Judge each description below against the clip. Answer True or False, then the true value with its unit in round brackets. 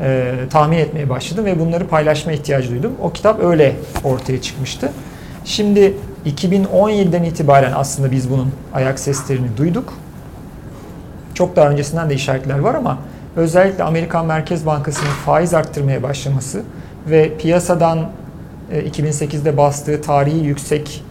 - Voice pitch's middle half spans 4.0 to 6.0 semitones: False (3.2 semitones)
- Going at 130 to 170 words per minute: False (120 wpm)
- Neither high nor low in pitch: True (150 Hz)